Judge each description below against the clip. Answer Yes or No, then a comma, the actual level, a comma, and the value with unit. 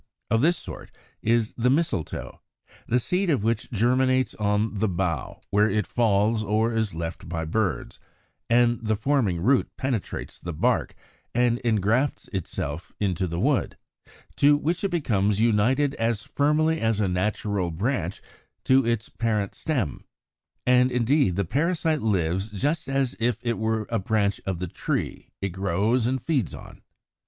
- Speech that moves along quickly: No, average, 155 wpm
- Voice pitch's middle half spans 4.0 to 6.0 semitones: Yes, average, 4.6 semitones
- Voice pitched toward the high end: No, low, 110 Hz